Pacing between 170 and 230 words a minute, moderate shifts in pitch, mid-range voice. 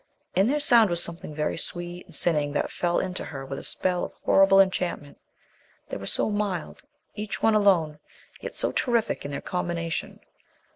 Yes: average, 180 wpm; average, 4.1 semitones; medium, 175 Hz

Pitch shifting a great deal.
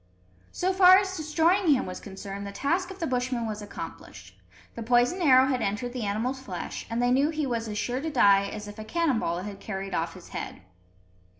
Yes: wide, 7.0 semitones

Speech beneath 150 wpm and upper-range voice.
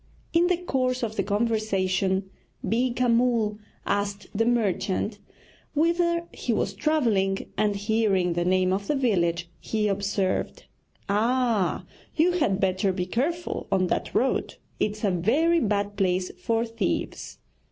Yes: slow, 135 wpm; high, 210 Hz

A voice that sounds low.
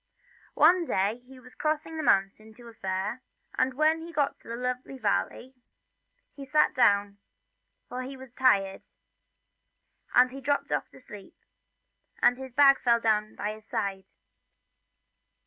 No: very high, 250 Hz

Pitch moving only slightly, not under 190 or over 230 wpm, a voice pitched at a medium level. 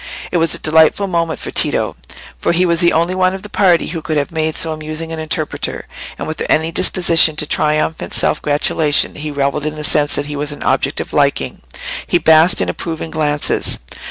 Yes: narrow, 1.9 semitones; fast, 205 wpm; medium, 160 Hz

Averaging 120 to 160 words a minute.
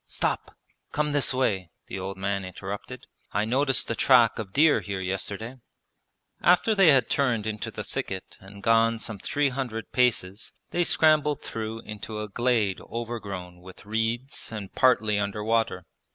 Yes: average, 155 wpm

